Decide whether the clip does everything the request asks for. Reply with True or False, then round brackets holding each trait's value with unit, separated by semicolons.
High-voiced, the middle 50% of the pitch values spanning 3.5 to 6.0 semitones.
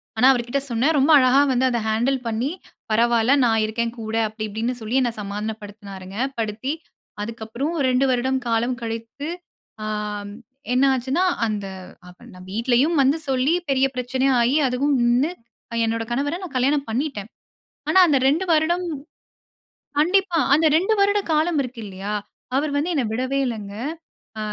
True (250 Hz; 4.0 semitones)